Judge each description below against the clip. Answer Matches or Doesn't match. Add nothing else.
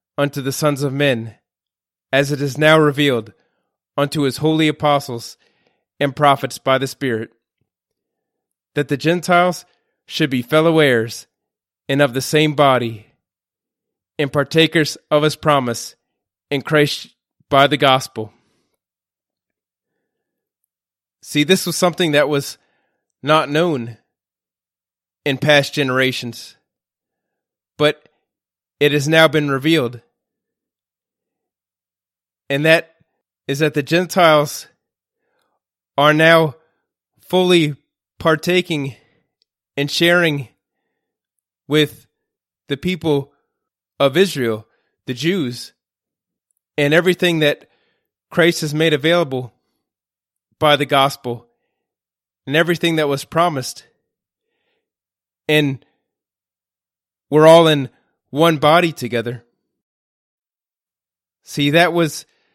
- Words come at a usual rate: Doesn't match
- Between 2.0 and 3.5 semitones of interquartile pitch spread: Doesn't match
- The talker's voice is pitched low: Doesn't match